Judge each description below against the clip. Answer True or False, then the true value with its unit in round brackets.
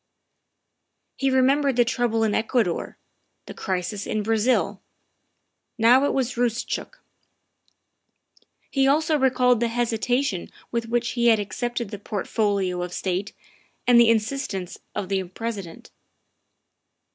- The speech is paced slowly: True (120 wpm)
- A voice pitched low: False (230 Hz)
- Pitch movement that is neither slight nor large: True (3.5 semitones)